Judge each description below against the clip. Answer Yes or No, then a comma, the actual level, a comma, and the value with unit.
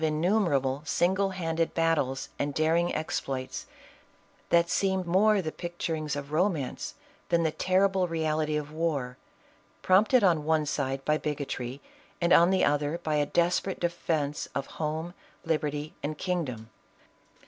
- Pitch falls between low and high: Yes, medium, 160 Hz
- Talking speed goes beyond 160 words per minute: No, average, 140 wpm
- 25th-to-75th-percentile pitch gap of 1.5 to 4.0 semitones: Yes, average, 2.9 semitones